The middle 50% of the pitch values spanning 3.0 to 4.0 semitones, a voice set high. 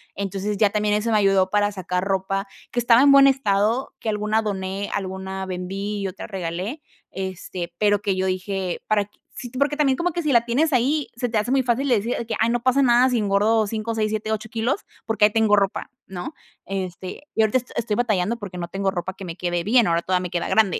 Yes: average, 3.7 semitones; high, 210 Hz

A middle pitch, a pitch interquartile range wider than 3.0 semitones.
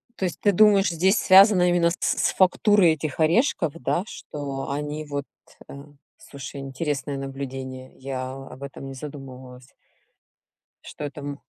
Yes: medium, 145 Hz; average, 4.4 semitones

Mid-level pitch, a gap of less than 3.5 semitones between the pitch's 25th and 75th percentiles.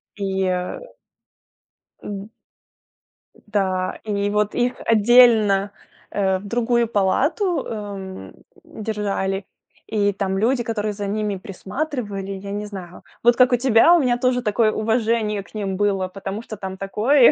No: high, 210 Hz; average, 3.1 semitones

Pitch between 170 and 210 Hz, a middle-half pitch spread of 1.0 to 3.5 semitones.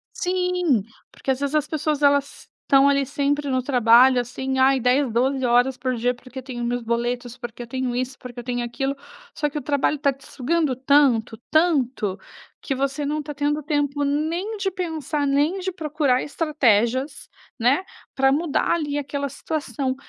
No: very high, 275 Hz; average, 3.0 semitones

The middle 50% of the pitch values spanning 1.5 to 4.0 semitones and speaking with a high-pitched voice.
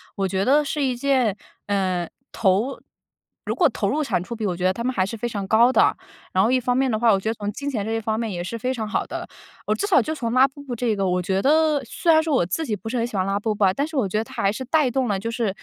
No: average, 4.8 semitones; high, 230 Hz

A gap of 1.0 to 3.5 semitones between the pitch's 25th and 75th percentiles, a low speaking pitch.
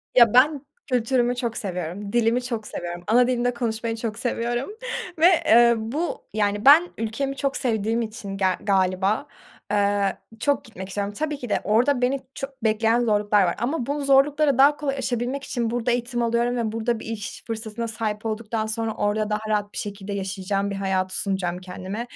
No: average, 3.2 semitones; high, 225 Hz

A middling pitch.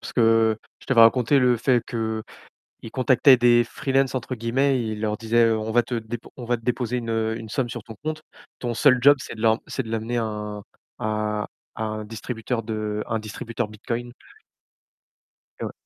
No: low, 115 Hz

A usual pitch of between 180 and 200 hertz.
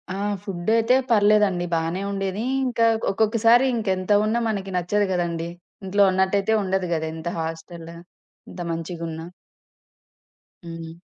Yes: high, 190 Hz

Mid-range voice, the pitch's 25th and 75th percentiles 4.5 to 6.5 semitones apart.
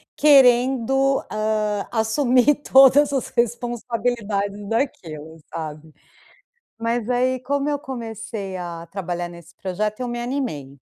No: high, 230 Hz; average, 4.8 semitones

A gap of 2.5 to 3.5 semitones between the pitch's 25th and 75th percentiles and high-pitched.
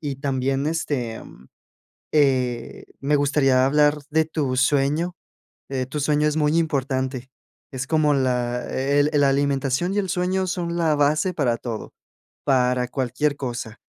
No: average, 2.8 semitones; medium, 140 Hz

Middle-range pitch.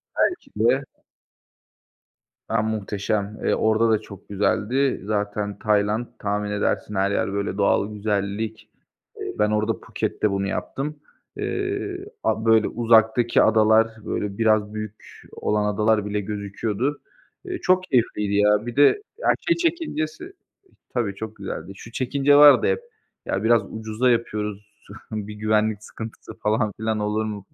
No: low, 110 Hz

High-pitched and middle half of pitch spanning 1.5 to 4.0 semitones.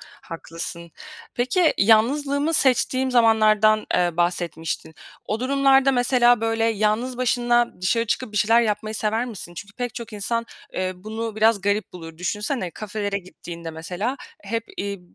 Yes: high, 220 Hz; average, 3.6 semitones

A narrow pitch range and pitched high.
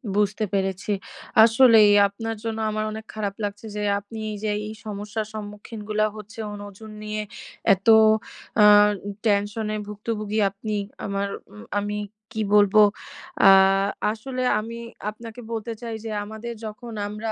Yes: narrow, 1.4 semitones; high, 215 Hz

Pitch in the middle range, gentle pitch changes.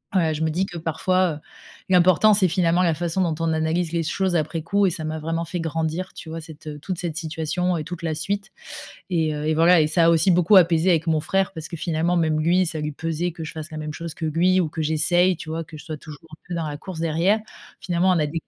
Yes: medium, 165 Hz; narrow, 2.1 semitones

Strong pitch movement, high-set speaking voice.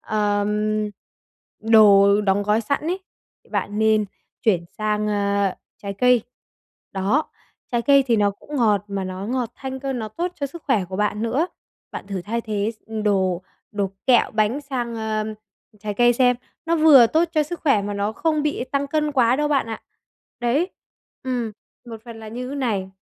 No: average, 4.4 semitones; high, 225 Hz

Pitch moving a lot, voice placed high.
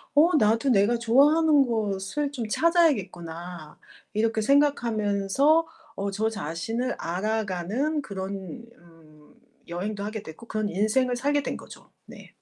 Yes: wide, 6.0 semitones; high, 220 Hz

